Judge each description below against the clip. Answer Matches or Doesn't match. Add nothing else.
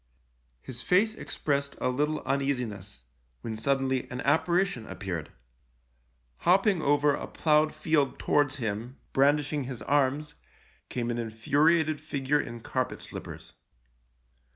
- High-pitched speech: Doesn't match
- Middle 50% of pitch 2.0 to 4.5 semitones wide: Matches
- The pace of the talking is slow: Matches